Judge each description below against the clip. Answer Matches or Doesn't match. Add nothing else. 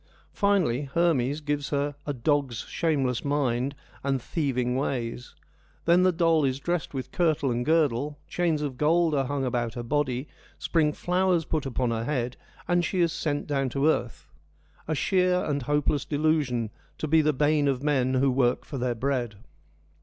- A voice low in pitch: Doesn't match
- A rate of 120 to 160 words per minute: Doesn't match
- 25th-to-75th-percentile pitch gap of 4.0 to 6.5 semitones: Doesn't match